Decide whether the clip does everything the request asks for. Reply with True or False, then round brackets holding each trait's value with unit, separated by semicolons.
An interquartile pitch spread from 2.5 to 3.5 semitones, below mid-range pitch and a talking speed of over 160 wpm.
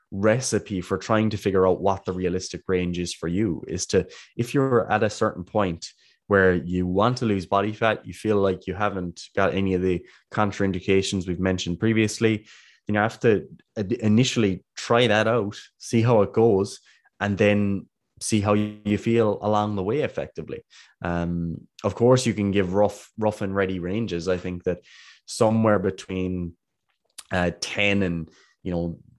True (2.9 semitones; 100 Hz; 175 wpm)